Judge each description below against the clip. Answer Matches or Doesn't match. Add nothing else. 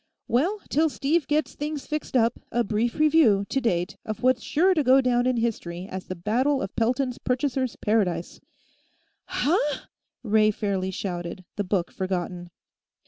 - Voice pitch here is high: Matches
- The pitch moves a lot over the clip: Matches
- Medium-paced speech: Matches